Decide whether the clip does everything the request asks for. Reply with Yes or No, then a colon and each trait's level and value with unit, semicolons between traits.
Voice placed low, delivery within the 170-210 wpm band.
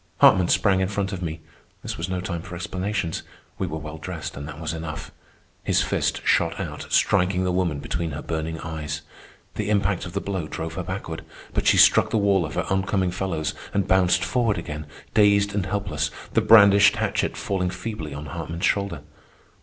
Yes: very low, 90 Hz; average, 195 wpm